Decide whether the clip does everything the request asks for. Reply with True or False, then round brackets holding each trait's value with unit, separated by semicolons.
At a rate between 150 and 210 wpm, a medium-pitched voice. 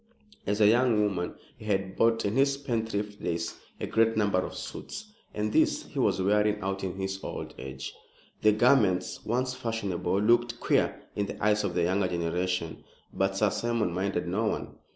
False (180 wpm; 105 Hz)